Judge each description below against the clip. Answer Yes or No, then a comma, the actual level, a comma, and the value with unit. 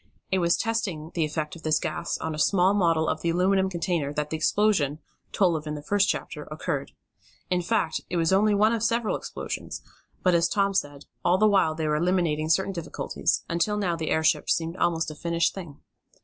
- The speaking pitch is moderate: Yes, medium, 170 Hz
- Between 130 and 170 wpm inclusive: No, fast, 205 wpm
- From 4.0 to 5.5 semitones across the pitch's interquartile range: No, average, 3.6 semitones